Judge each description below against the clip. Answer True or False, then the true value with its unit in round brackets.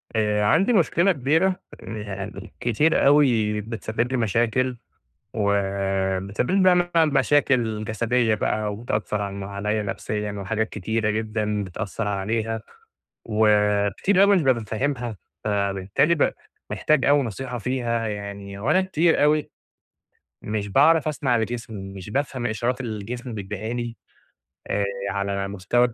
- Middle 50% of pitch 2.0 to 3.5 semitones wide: False (4.0 semitones)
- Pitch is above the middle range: False (110 Hz)